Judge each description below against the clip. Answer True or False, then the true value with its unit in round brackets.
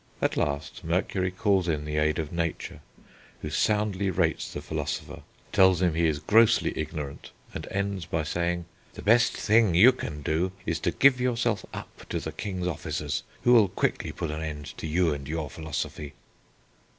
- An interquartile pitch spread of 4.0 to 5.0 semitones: True (4.4 semitones)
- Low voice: True (85 Hz)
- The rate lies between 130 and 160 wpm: False (175 wpm)